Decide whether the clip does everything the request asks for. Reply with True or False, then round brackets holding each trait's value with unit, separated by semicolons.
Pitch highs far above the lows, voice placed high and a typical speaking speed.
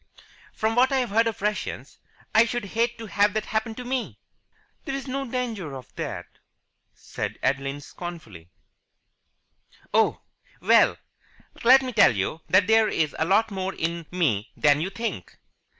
True (6.3 semitones; 210 Hz; 155 wpm)